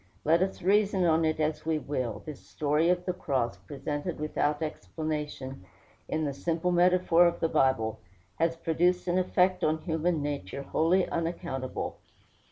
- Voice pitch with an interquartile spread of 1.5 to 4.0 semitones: Yes, average, 3.2 semitones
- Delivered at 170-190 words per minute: No, average, 155 wpm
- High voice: No, medium, 160 Hz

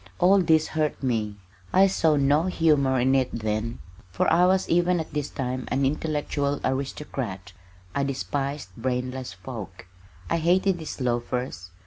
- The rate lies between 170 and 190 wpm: No, average, 145 wpm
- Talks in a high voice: No, medium, 140 Hz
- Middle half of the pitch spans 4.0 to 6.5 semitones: Yes, average, 4.3 semitones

